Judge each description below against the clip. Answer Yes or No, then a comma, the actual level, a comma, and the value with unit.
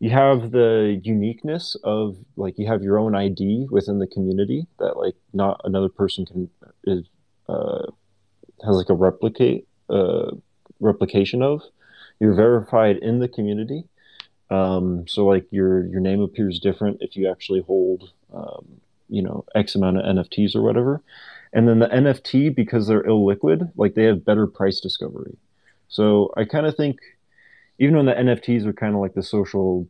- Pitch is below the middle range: Yes, low, 105 Hz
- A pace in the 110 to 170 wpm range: Yes, average, 165 wpm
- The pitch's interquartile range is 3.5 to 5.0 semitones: Yes, average, 3.8 semitones